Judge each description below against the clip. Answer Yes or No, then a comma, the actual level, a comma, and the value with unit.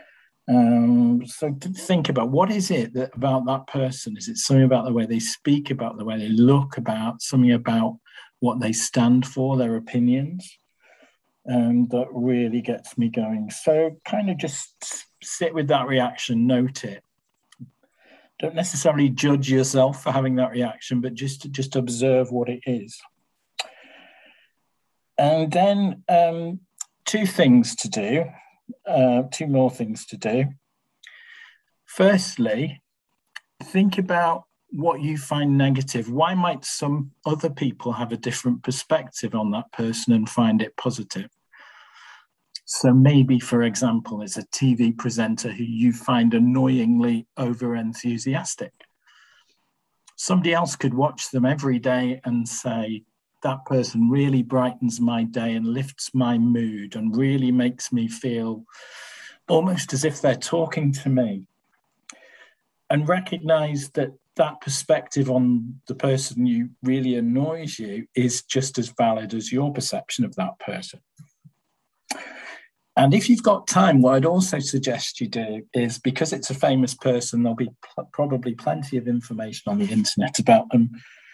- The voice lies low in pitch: Yes, low, 130 Hz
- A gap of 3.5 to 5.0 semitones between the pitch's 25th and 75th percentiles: Yes, average, 4.2 semitones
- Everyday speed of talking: Yes, average, 145 wpm